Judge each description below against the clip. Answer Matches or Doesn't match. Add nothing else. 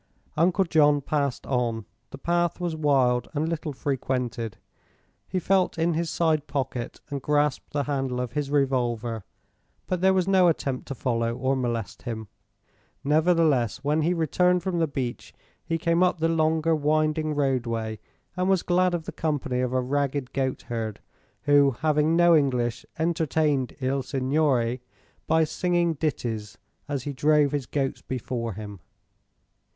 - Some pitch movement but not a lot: Matches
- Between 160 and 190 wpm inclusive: Doesn't match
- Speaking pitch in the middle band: Matches